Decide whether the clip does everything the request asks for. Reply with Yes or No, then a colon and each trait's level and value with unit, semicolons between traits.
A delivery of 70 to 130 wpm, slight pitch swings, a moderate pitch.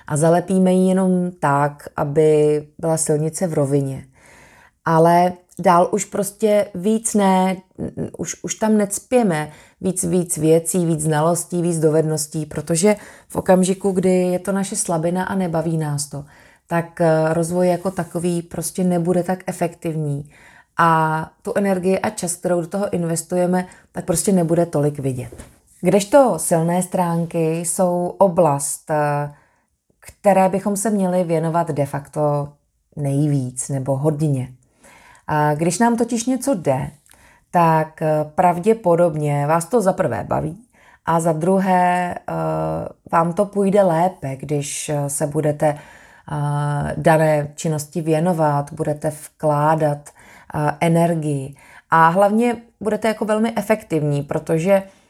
No: average, 120 wpm; average, 3.7 semitones; medium, 170 Hz